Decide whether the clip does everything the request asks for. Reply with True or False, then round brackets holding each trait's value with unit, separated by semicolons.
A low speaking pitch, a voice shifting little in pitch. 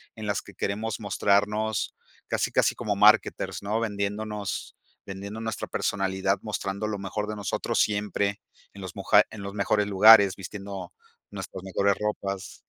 True (100 Hz; 1.3 semitones)